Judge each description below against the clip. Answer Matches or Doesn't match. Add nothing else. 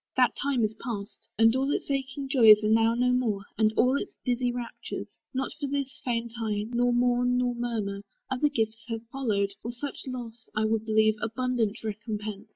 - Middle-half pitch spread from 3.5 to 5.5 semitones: Doesn't match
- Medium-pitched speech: Doesn't match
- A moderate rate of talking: Matches